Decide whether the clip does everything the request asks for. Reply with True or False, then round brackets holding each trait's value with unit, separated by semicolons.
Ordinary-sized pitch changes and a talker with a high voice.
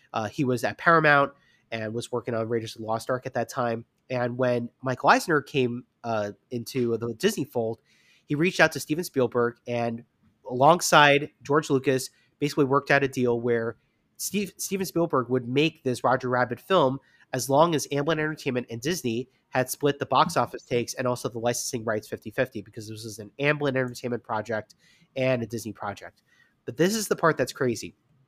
False (3.5 semitones; 125 Hz)